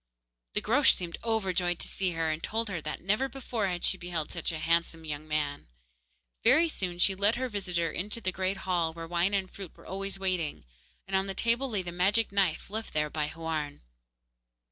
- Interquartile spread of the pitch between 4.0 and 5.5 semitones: No, average, 3.5 semitones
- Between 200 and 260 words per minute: Yes, fast, 205 wpm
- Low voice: No, medium, 185 Hz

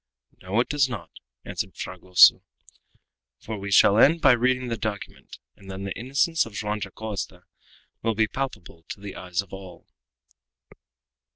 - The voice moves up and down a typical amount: Yes, average, 4.2 semitones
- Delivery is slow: No, average, 155 wpm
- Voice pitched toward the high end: No, low, 105 Hz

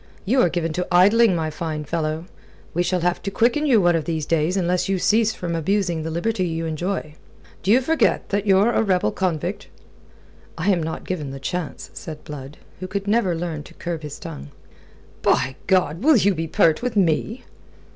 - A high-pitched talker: No, medium, 175 Hz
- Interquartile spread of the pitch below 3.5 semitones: No, average, 3.8 semitones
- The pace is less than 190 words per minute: No, average, 195 wpm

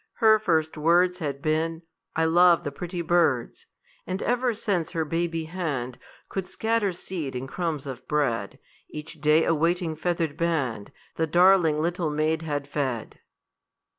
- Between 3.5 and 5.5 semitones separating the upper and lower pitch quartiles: No, average, 2.9 semitones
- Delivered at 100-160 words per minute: Yes, average, 150 wpm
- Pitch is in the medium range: Yes, medium, 160 Hz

